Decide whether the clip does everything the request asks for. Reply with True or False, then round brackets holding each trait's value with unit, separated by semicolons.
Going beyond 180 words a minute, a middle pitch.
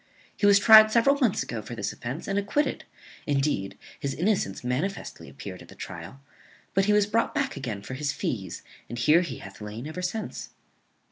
True (190 wpm; 155 Hz)